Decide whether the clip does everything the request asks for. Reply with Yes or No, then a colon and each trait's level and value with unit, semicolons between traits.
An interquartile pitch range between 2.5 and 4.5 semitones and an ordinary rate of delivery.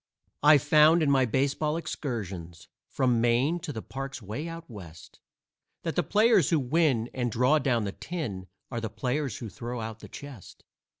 No: average, 5.2 semitones; average, 175 wpm